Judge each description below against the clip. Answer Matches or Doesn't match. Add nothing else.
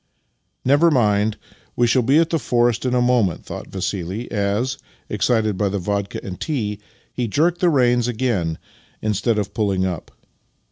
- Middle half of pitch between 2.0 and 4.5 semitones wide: Matches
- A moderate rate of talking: Matches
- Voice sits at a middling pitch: Doesn't match